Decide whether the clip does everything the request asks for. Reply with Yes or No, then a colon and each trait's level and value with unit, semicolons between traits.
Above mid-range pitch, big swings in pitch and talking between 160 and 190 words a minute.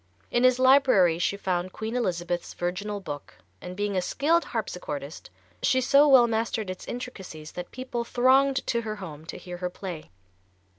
Yes: high, 205 Hz; wide, 5.9 semitones; average, 165 wpm